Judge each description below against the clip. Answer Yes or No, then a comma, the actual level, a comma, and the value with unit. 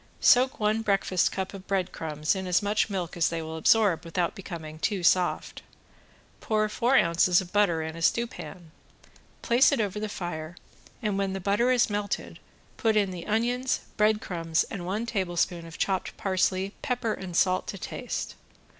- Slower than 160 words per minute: No, average, 170 wpm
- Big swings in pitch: No, average, 3.6 semitones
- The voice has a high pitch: Yes, high, 195 Hz